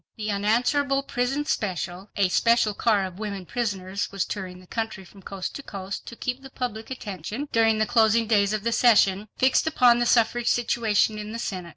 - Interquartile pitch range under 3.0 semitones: No, average, 3.3 semitones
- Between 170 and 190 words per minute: Yes, average, 185 wpm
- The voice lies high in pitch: Yes, high, 215 Hz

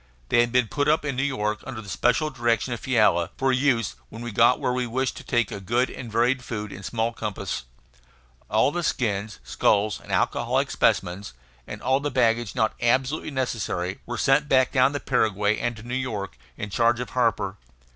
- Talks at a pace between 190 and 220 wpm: Yes, average, 195 wpm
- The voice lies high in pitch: No, low, 120 Hz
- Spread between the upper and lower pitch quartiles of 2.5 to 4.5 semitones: Yes, average, 3.4 semitones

